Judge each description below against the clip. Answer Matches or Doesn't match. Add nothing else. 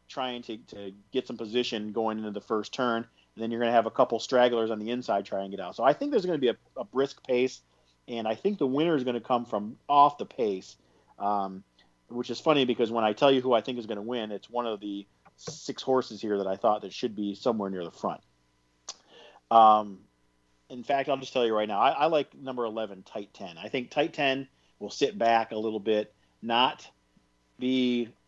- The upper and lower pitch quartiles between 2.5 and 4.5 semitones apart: Matches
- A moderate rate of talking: Doesn't match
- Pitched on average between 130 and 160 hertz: Doesn't match